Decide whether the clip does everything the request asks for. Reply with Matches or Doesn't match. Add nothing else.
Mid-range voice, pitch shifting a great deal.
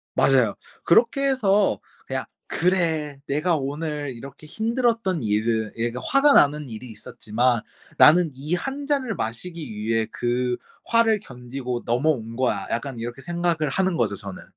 Matches